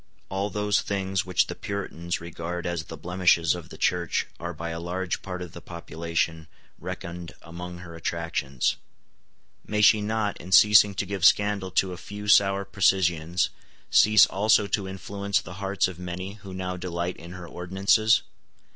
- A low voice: Yes, very low, 90 Hz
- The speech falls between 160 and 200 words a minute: Yes, average, 165 wpm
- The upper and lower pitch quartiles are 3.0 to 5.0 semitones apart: No, narrow, 2.6 semitones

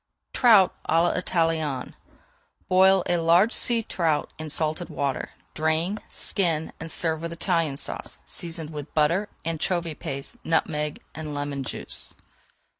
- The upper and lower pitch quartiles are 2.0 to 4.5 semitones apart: Yes, narrow, 2.4 semitones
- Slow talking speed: Yes, slow, 125 wpm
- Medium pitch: Yes, medium, 165 Hz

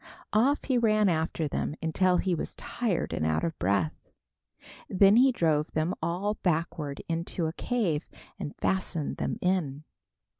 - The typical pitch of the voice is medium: Yes, medium, 170 Hz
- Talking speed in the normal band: Yes, average, 150 wpm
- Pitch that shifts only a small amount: No, average, 4.3 semitones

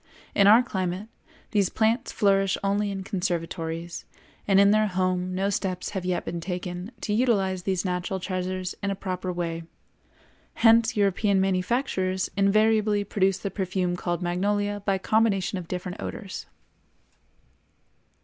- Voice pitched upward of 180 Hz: Yes, high, 190 Hz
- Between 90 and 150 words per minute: Yes, average, 140 wpm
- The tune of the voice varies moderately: No, narrow, 2.0 semitones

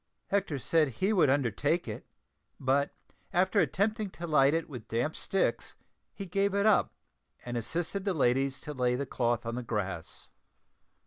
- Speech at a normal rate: Yes, average, 165 wpm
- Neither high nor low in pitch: Yes, medium, 145 Hz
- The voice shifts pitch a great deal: Yes, wide, 7.4 semitones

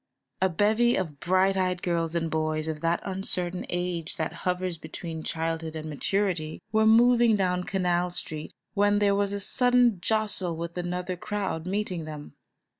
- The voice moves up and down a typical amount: Yes, average, 3.5 semitones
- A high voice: No, medium, 180 Hz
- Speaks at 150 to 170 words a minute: Yes, average, 160 wpm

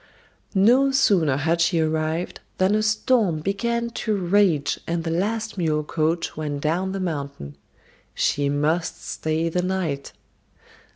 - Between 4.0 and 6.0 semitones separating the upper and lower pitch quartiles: Yes, average, 4.3 semitones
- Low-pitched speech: No, medium, 170 Hz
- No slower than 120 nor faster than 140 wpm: Yes, slow, 135 wpm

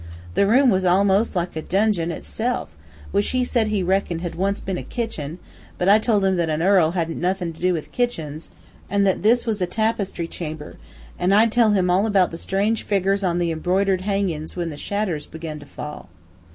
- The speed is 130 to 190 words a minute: No, fast, 205 wpm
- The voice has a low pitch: No, high, 190 Hz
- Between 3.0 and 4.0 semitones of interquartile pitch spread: Yes, average, 3.5 semitones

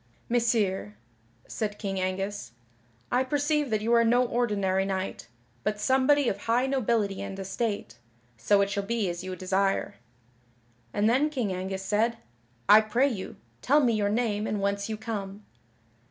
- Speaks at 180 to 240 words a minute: No, average, 155 wpm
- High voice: Yes, high, 210 Hz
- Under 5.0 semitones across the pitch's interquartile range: Yes, average, 3.5 semitones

